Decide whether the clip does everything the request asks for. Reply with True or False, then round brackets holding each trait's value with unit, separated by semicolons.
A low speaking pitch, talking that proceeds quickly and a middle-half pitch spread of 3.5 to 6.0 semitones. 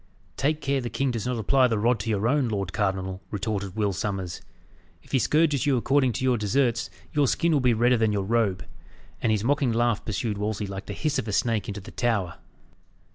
True (115 Hz; 220 wpm; 4.1 semitones)